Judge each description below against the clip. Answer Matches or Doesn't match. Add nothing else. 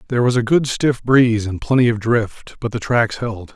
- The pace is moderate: Doesn't match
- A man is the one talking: Matches